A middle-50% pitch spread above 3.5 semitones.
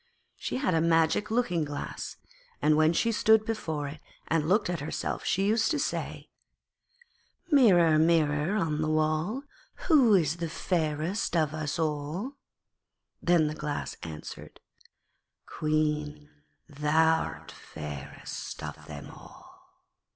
Yes: average, 3.9 semitones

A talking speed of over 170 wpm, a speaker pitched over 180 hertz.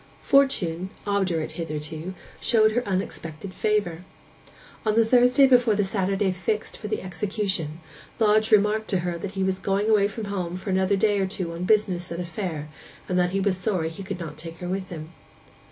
Yes: average, 190 wpm; high, 190 Hz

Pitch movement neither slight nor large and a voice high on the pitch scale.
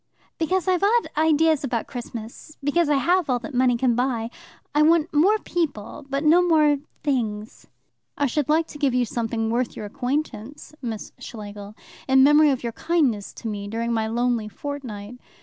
Yes: average, 5.0 semitones; very high, 265 Hz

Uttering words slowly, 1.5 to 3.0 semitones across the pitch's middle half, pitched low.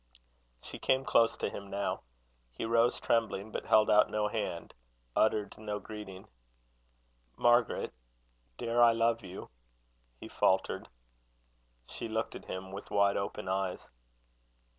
Yes: slow, 130 wpm; average, 2.7 semitones; low, 105 Hz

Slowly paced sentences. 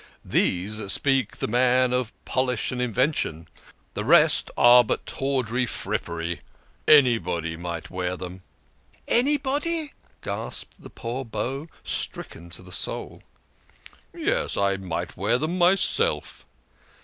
Yes: slow, 125 wpm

